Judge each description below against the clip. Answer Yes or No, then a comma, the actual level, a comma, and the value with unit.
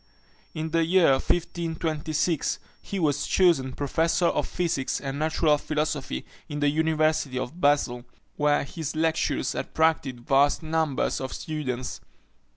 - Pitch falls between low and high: Yes, medium, 155 Hz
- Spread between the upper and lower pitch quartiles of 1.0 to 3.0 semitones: Yes, narrow, 2.5 semitones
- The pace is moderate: No, slow, 125 wpm